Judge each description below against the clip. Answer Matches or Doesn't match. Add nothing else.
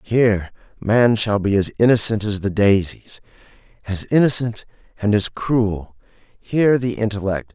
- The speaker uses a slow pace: Matches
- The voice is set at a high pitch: Doesn't match